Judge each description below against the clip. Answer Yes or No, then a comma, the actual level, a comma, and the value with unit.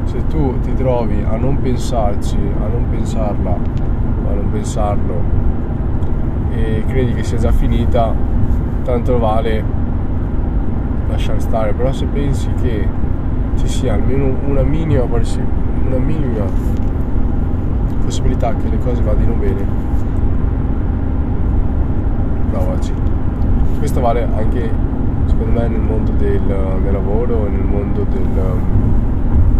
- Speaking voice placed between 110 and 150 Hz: No, low, 100 Hz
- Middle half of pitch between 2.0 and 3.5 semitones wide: No, average, 4.8 semitones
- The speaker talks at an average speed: No, slow, 110 wpm